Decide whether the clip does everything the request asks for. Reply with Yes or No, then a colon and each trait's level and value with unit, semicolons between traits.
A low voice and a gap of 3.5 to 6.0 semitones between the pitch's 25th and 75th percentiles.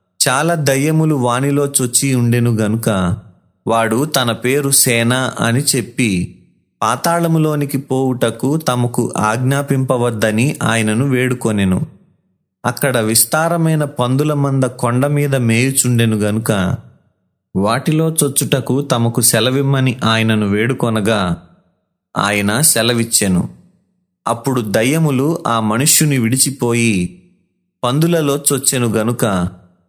Yes: low, 125 Hz; average, 3.9 semitones